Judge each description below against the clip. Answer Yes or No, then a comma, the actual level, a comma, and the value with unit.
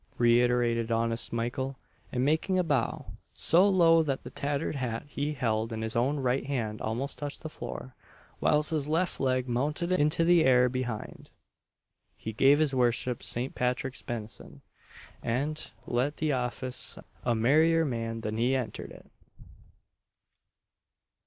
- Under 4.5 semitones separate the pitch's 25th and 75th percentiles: Yes, average, 4.0 semitones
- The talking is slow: No, average, 145 wpm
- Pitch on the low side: Yes, low, 130 Hz